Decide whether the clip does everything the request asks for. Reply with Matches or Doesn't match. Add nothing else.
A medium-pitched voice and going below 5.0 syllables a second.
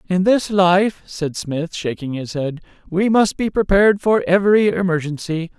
Matches